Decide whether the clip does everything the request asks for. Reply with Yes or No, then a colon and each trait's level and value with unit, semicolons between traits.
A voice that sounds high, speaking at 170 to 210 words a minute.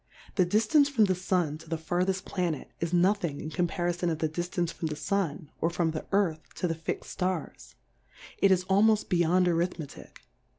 No: medium, 175 Hz; average, 180 wpm